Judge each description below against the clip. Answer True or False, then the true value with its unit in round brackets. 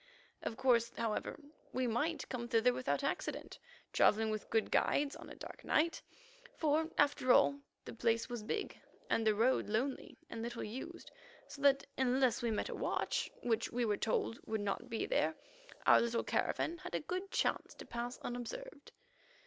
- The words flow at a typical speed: True (175 wpm)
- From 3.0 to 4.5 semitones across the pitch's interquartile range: True (3.9 semitones)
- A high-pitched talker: True (245 Hz)